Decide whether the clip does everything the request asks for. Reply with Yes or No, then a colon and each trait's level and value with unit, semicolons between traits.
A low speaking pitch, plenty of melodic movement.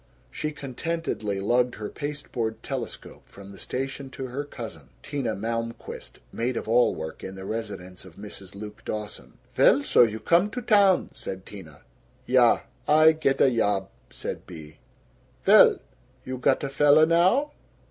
Yes: low, 120 Hz; wide, 6.0 semitones